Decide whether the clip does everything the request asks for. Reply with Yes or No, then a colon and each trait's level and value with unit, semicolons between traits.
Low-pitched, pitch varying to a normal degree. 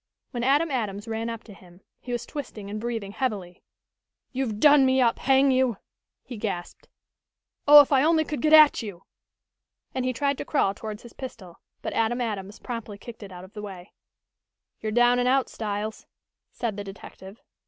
No: high, 230 Hz; average, 4.3 semitones